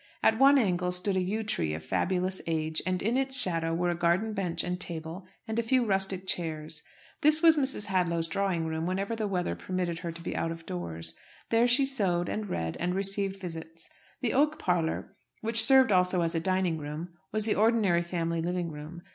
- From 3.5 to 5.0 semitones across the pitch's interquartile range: Yes, average, 4.4 semitones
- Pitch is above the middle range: No, medium, 180 Hz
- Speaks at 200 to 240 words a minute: Yes, fast, 205 wpm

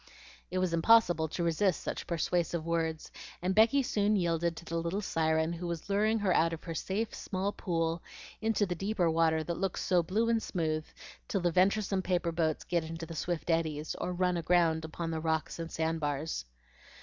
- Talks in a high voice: No, medium, 170 Hz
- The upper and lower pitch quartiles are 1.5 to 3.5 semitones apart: Yes, narrow, 2.6 semitones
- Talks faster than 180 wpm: Yes, average, 190 wpm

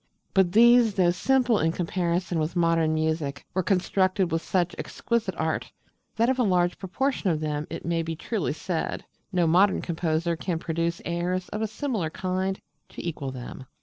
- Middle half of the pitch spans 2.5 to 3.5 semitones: Yes, average, 2.9 semitones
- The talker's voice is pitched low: No, medium, 175 Hz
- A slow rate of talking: No, average, 175 wpm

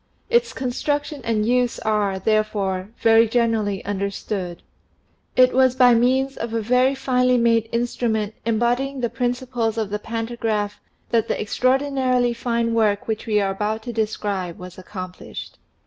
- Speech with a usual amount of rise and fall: Yes, average, 3.0 semitones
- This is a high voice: Yes, high, 230 Hz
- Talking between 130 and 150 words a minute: Yes, average, 145 wpm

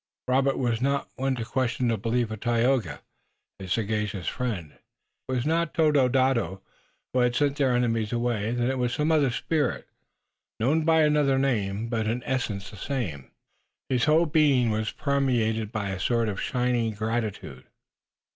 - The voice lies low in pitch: Yes, low, 120 Hz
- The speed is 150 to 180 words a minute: Yes, average, 165 wpm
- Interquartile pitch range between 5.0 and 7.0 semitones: No, average, 3.6 semitones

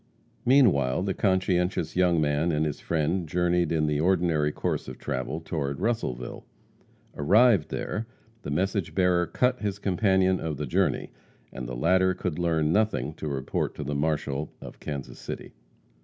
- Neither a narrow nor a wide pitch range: Yes, average, 4.0 semitones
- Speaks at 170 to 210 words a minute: No, average, 155 wpm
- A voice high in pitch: No, very low, 85 Hz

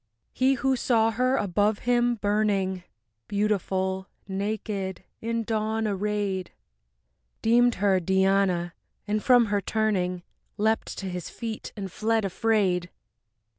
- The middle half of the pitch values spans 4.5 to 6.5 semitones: No, average, 2.8 semitones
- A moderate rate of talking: No, slow, 115 wpm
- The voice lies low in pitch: No, high, 205 Hz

